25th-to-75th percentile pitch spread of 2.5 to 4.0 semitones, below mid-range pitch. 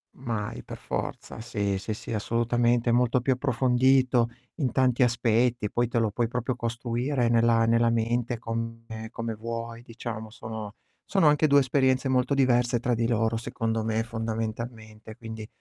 No: narrow, 1.6 semitones; low, 115 Hz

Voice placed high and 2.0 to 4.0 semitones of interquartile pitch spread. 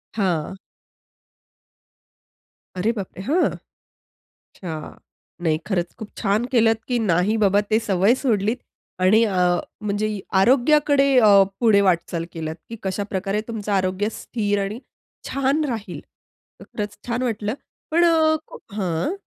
Yes: high, 210 Hz; average, 3.7 semitones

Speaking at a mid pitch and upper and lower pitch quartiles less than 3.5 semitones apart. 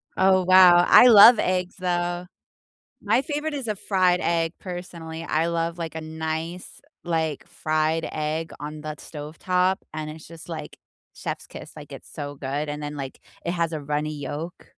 Yes: medium, 165 Hz; average, 2.8 semitones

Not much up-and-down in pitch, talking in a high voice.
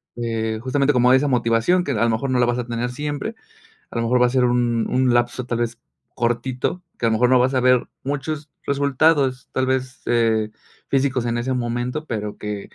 No: narrow, 2.0 semitones; low, 125 Hz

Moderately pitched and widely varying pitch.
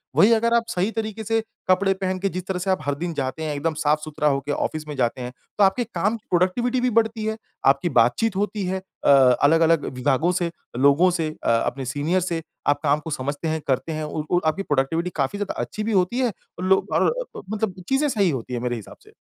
Yes: medium, 170 Hz; wide, 5.7 semitones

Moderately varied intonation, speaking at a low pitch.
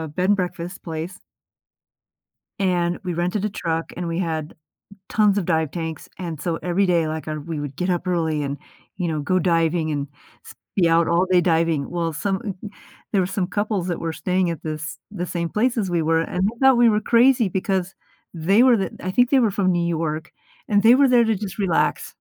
No: average, 3.3 semitones; medium, 175 Hz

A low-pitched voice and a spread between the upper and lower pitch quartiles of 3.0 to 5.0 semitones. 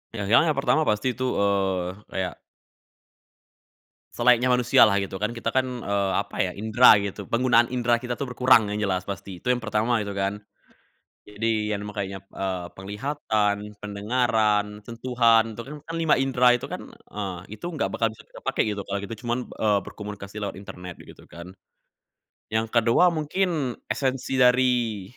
Yes: low, 110 Hz; average, 3.7 semitones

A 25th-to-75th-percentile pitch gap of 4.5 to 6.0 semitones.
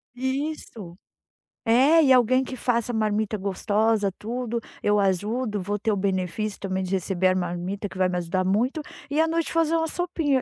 Yes: average, 5.3 semitones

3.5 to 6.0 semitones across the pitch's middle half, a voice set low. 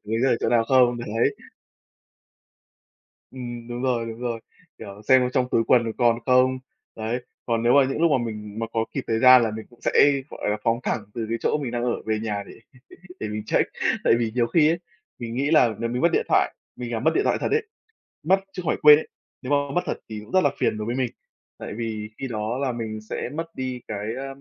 No: average, 2.7 semitones; low, 120 Hz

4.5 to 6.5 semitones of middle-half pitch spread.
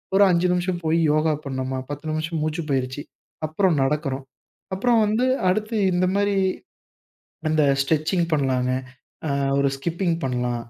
Yes: average, 4.8 semitones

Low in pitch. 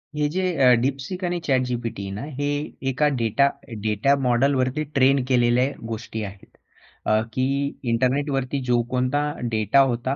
Yes: low, 130 Hz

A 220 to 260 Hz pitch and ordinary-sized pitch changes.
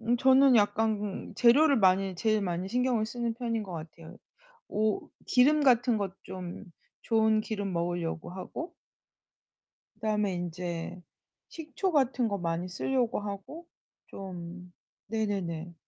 No: high, 210 Hz; average, 5.0 semitones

